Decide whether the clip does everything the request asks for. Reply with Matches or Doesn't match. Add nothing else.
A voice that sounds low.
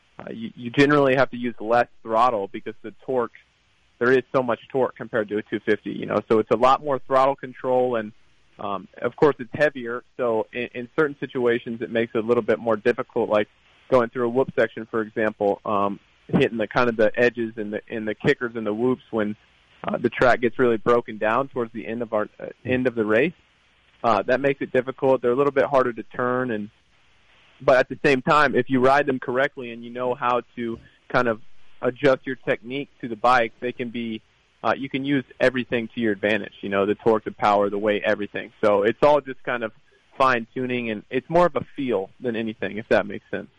Matches